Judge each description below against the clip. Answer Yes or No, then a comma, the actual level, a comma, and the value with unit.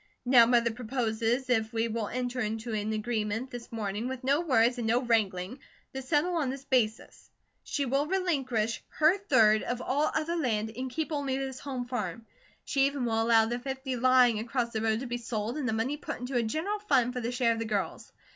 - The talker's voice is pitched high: Yes, high, 245 Hz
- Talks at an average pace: No, fast, 210 wpm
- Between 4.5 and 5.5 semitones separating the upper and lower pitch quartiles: No, average, 3.1 semitones